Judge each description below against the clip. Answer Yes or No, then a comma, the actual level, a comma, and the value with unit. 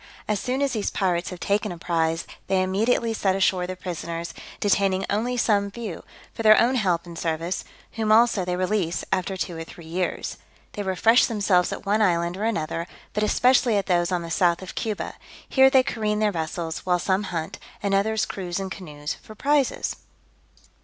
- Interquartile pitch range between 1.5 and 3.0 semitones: No, average, 3.7 semitones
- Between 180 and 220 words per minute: Yes, average, 190 wpm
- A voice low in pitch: No, high, 190 Hz